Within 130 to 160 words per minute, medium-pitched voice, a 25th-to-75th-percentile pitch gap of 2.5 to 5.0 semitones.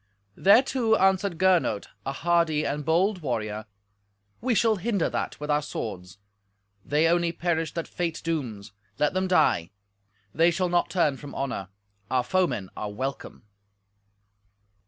No: slow, 135 wpm; medium, 165 Hz; wide, 5.4 semitones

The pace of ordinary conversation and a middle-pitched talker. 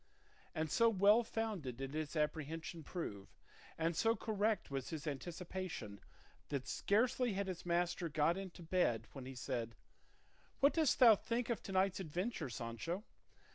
Yes: average, 150 wpm; medium, 175 Hz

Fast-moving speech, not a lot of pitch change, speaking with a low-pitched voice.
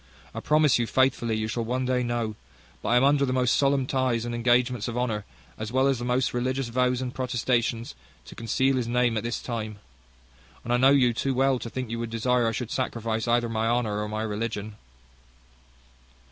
Yes: fast, 210 wpm; narrow, 2.0 semitones; low, 120 Hz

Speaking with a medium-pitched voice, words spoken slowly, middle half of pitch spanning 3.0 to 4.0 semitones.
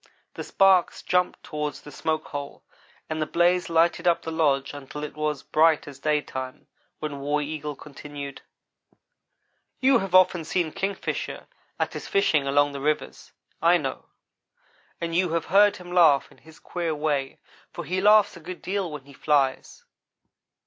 No: medium, 155 Hz; average, 165 wpm; average, 3.4 semitones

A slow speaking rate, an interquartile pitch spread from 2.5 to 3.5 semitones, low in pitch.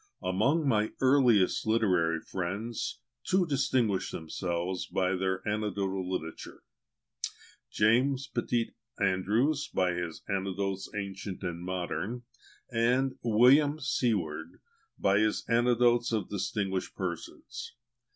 No: slow, 100 wpm; average, 4.5 semitones; low, 105 Hz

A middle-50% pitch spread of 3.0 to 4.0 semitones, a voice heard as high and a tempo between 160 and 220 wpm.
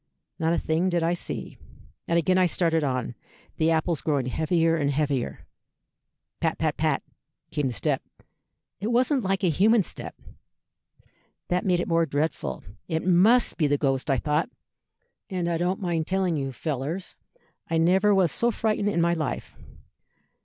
No: average, 3.5 semitones; medium, 170 Hz; average, 165 wpm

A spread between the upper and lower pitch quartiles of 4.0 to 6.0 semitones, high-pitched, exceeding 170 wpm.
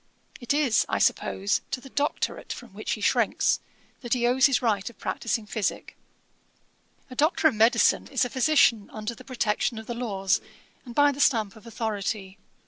No: average, 3.5 semitones; high, 235 Hz; average, 180 wpm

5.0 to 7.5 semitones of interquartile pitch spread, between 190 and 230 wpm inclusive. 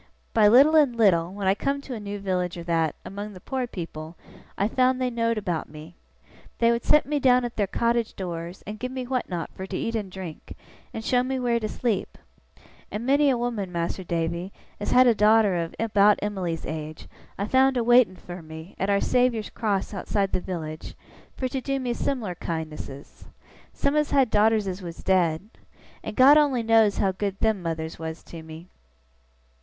Yes: wide, 5.6 semitones; fast, 205 wpm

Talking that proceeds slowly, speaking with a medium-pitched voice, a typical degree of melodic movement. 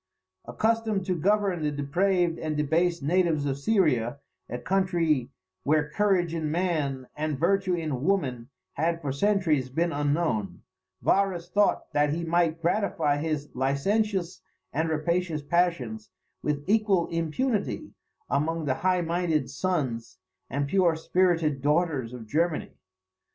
Yes: slow, 130 wpm; medium, 165 Hz; average, 4.0 semitones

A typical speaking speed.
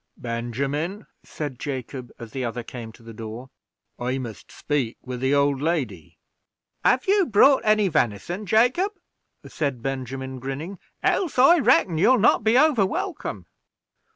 Yes: average, 145 wpm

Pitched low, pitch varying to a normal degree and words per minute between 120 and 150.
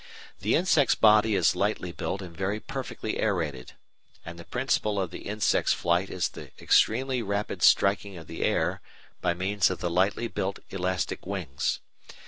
No: low, 100 Hz; average, 3.4 semitones; average, 160 wpm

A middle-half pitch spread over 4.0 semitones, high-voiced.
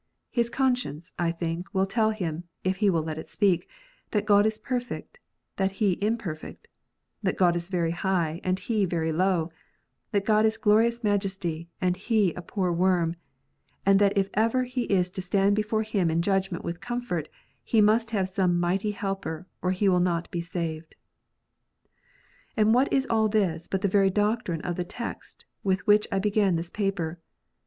No: average, 3.5 semitones; high, 195 Hz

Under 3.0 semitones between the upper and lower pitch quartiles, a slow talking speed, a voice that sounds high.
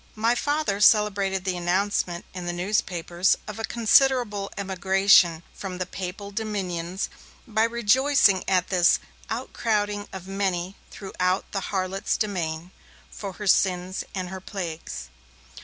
Yes: narrow, 2.5 semitones; slow, 125 wpm; high, 195 Hz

